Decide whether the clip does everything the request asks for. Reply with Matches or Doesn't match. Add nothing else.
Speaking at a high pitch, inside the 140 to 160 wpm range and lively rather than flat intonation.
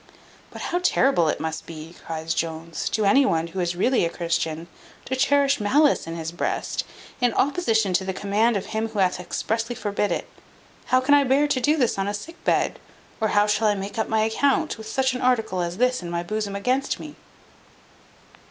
Doesn't match